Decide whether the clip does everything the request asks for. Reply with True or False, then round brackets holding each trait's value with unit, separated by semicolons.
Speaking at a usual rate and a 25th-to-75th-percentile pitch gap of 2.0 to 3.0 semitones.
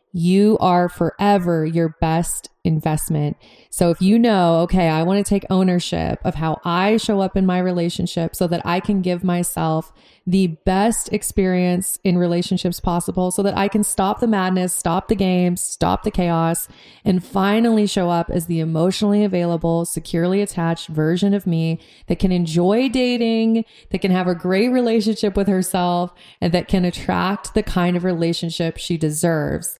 True (170 wpm; 2.6 semitones)